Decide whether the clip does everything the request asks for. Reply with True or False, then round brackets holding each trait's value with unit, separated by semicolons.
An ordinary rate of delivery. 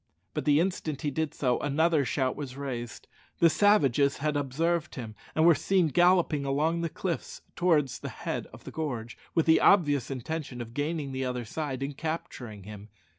True (180 wpm)